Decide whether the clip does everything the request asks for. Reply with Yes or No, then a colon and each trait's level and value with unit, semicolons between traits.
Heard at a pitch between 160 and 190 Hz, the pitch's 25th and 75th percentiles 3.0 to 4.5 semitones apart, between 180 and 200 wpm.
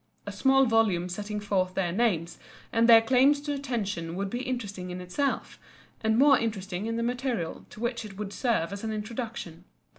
No: high, 220 Hz; average, 4.0 semitones; average, 185 wpm